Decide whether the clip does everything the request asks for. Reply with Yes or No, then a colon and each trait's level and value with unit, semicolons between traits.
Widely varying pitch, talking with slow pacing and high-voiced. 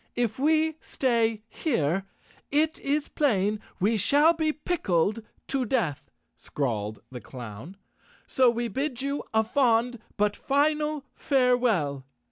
Yes: wide, 6.5 semitones; slow, 120 wpm; high, 240 Hz